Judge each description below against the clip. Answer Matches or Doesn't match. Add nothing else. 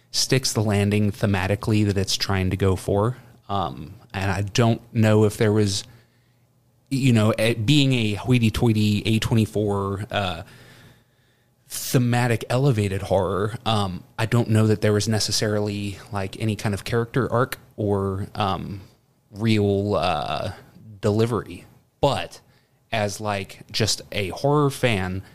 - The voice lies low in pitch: Matches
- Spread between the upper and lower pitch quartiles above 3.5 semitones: Doesn't match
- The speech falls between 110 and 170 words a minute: Matches